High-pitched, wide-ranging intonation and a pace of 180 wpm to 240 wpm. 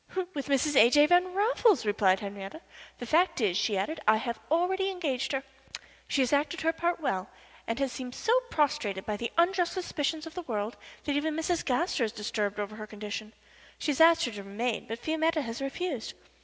Yes: very high, 275 Hz; wide, 7.2 semitones; average, 200 wpm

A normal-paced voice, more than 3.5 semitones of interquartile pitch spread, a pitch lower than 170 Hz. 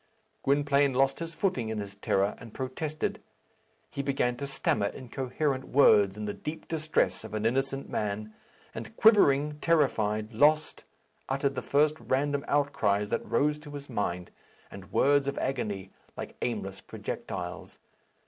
Yes: average, 145 wpm; average, 5.1 semitones; low, 135 Hz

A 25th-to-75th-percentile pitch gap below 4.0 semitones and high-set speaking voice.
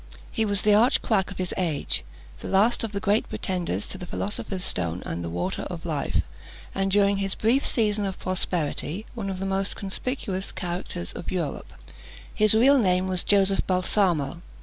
Yes: narrow, 2.5 semitones; high, 195 Hz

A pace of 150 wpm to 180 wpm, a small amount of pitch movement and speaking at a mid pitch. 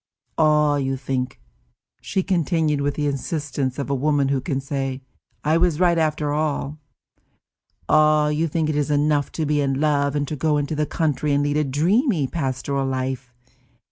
Yes: average, 175 wpm; narrow, 1.9 semitones; medium, 145 Hz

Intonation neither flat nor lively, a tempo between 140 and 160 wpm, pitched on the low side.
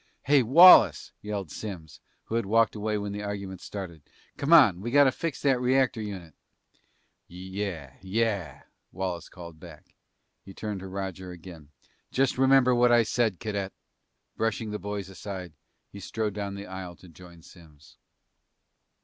Yes: average, 3.8 semitones; average, 150 wpm; low, 100 Hz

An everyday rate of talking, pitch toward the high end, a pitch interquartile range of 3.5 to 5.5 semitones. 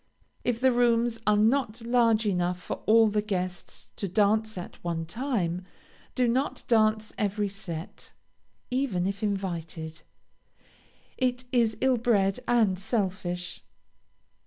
No: slow, 125 wpm; high, 215 Hz; average, 4.3 semitones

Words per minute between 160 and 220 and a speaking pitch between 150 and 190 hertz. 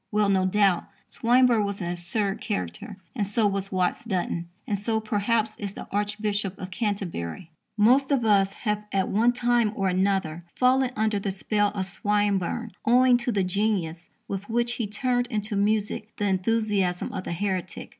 No: average, 170 wpm; high, 205 Hz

